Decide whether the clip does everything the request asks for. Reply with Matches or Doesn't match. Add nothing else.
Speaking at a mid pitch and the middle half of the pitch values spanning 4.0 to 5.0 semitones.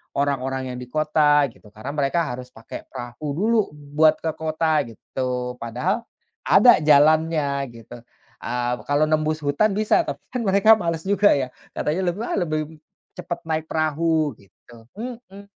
Matches